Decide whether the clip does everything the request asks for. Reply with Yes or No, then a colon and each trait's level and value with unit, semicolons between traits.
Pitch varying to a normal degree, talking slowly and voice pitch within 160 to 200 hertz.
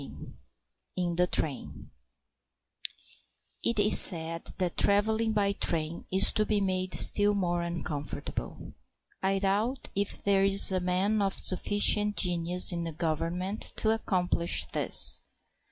Yes: average, 3.0 semitones; slow, 130 wpm; high, 190 Hz